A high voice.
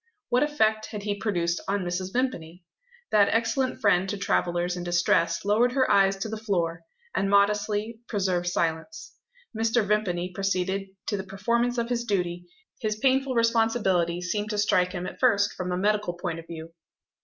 Yes: high, 200 Hz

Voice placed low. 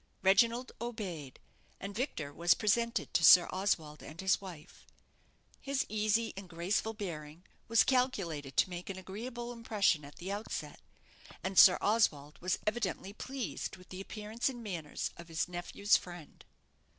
No: high, 195 Hz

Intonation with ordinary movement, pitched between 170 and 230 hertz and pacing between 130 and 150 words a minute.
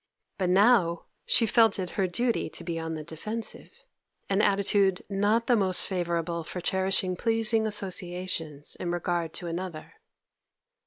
Yes: average, 3.4 semitones; medium, 185 Hz; average, 145 wpm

